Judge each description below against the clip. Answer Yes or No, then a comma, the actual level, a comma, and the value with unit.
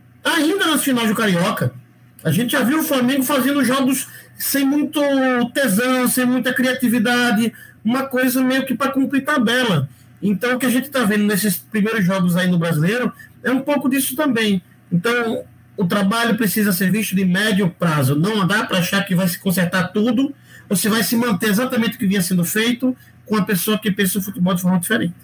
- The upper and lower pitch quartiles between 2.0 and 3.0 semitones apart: No, average, 4.9 semitones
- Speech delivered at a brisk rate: Yes, fast, 195 wpm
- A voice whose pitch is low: No, high, 225 Hz